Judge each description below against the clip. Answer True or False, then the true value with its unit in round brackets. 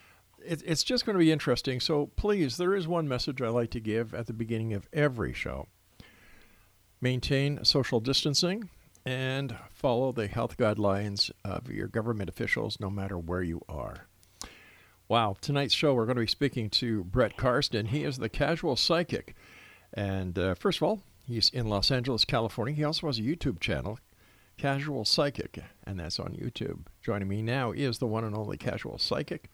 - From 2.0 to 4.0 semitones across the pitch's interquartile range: False (5.2 semitones)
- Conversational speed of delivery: True (175 wpm)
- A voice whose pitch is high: False (120 Hz)